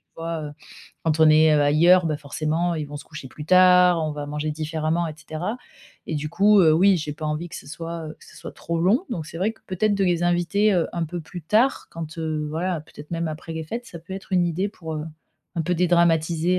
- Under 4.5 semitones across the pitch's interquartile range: Yes, narrow, 2.6 semitones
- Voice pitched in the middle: Yes, medium, 165 Hz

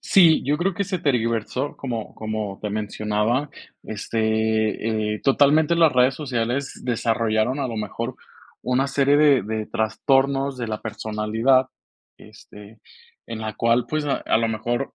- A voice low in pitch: Yes, low, 120 Hz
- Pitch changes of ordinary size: Yes, average, 4.0 semitones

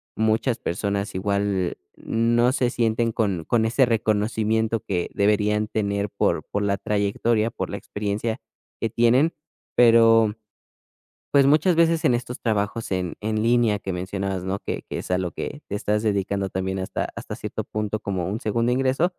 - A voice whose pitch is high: No, low, 110 Hz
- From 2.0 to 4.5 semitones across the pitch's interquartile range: Yes, narrow, 2.6 semitones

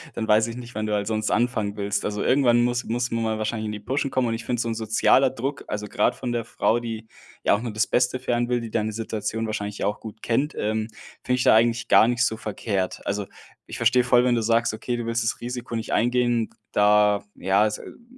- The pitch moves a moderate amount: No, narrow, 2.1 semitones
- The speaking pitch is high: No, low, 115 Hz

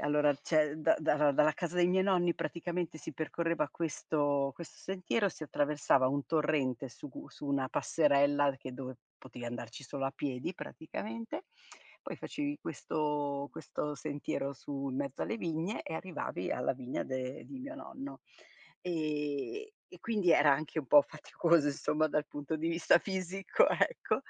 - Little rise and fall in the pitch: No, average, 3.5 semitones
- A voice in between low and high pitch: Yes, medium, 150 Hz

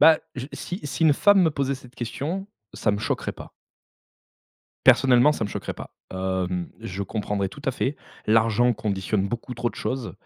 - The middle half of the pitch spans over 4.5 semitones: Yes, average, 5.3 semitones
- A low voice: Yes, low, 120 Hz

